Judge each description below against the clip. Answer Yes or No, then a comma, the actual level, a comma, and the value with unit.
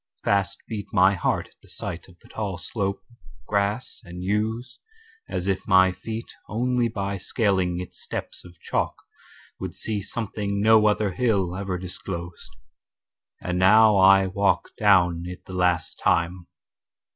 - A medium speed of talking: Yes, average, 150 wpm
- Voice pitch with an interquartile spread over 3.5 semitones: No, average, 2.7 semitones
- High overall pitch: No, low, 100 Hz